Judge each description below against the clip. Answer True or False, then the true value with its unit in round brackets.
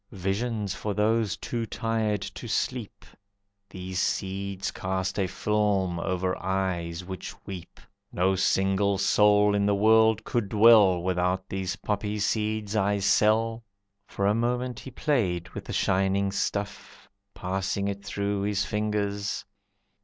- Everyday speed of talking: False (130 wpm)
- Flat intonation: True (2.0 semitones)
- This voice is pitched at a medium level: False (100 Hz)